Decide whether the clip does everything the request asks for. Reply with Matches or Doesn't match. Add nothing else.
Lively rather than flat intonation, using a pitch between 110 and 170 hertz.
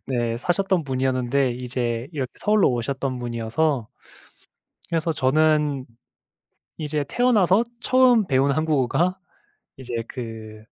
Doesn't match